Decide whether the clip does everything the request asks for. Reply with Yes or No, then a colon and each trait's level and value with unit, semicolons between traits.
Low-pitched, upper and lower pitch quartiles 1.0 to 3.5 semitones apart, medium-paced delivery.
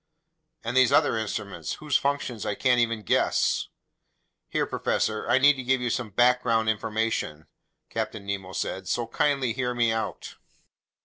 Yes: low, 115 Hz; narrow, 2.5 semitones; average, 150 wpm